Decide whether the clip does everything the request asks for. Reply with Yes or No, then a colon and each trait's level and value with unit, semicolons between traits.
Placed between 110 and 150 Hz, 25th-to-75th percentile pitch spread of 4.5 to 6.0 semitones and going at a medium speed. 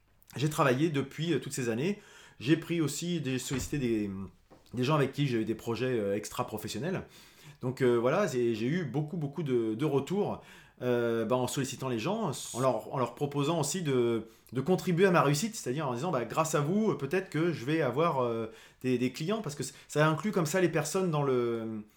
Yes: medium, 140 Hz; average, 5.2 semitones; average, 210 wpm